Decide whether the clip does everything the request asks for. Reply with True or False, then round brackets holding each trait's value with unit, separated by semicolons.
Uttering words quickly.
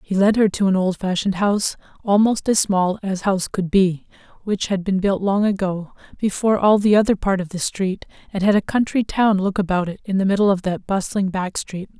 True (220 wpm)